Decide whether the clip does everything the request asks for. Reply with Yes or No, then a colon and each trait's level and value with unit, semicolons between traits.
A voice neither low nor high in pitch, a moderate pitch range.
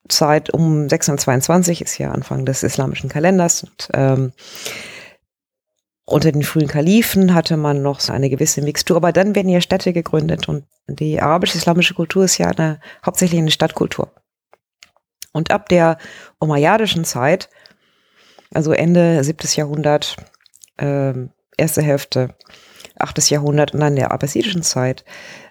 Yes: medium, 155 Hz; average, 3.6 semitones